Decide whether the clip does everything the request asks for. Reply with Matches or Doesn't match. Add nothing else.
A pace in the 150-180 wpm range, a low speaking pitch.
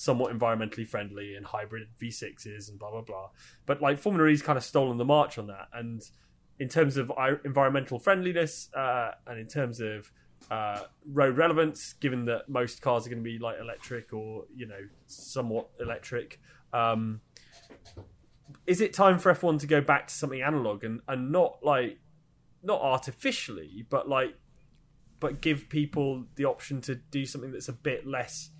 Matches